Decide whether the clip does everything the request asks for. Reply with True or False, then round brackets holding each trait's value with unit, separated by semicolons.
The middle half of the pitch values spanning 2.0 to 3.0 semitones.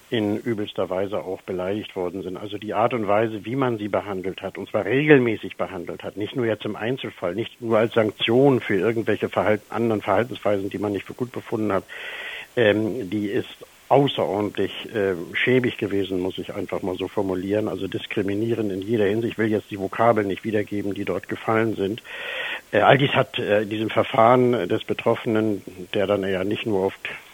True (2.5 semitones)